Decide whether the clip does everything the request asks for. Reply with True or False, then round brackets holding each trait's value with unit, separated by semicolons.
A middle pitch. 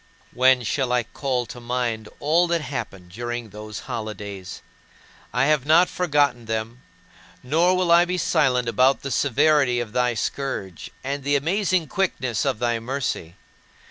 False (125 Hz)